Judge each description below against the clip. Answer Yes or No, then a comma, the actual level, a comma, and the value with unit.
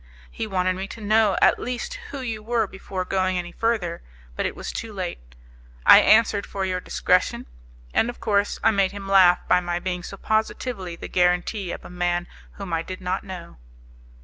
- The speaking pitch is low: No, high, 190 Hz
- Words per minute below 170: No, average, 195 wpm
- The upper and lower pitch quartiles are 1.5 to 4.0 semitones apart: Yes, average, 3.3 semitones